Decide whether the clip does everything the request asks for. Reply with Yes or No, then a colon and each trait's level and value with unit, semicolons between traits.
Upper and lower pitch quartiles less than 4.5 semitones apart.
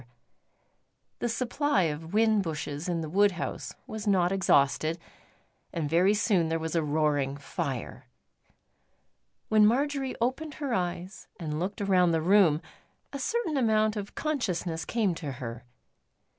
No: average, 5.3 semitones